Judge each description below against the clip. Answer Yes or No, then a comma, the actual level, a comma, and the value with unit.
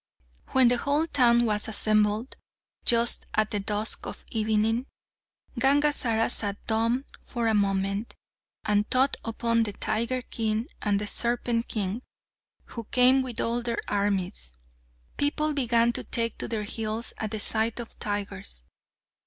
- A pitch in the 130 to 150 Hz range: No, high, 225 Hz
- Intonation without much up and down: Yes, narrow, 2.3 semitones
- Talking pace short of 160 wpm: Yes, average, 145 wpm